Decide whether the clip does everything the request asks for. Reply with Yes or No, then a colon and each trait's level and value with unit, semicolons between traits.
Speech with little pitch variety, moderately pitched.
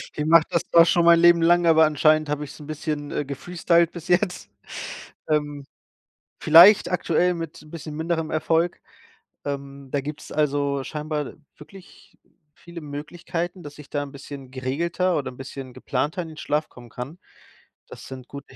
No: average, 3.0 semitones; medium, 155 Hz